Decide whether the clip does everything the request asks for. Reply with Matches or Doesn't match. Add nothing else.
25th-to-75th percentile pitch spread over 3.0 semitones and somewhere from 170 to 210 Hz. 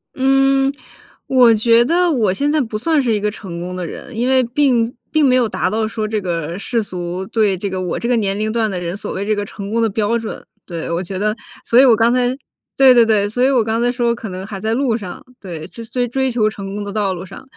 Doesn't match